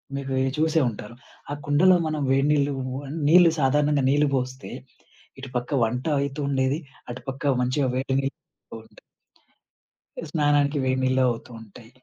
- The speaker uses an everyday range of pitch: No, narrow, 2.2 semitones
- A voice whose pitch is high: No, medium, 140 Hz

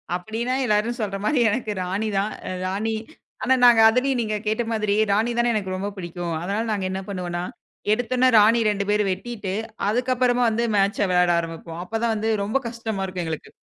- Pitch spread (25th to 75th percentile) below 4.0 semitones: Yes, average, 3.6 semitones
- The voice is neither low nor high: No, high, 210 Hz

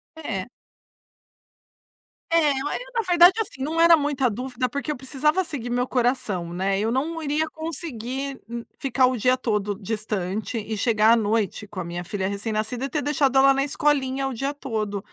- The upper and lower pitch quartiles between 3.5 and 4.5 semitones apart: No, average, 4.9 semitones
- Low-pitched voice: No, very high, 255 Hz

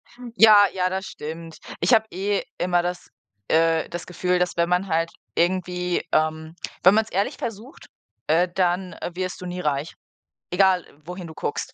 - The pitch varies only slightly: Yes, narrow, 2.3 semitones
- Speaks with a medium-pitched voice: Yes, medium, 180 Hz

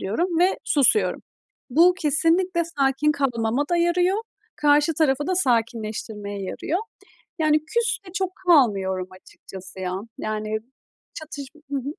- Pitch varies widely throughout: Yes, wide, 7.6 semitones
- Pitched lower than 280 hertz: No, very high, 290 Hz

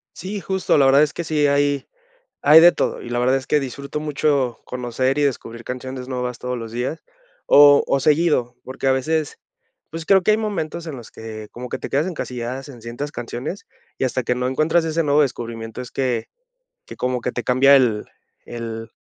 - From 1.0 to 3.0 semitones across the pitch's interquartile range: No, average, 3.5 semitones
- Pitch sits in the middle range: No, low, 130 Hz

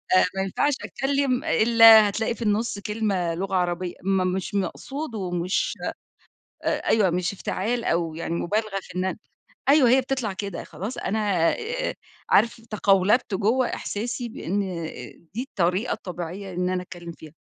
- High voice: Yes, high, 200 Hz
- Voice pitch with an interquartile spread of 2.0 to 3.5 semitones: No, average, 4.0 semitones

